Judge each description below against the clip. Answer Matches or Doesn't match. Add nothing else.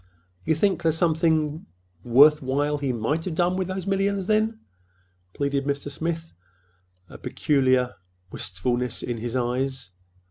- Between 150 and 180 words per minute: Doesn't match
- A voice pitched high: Doesn't match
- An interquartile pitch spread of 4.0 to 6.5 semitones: Matches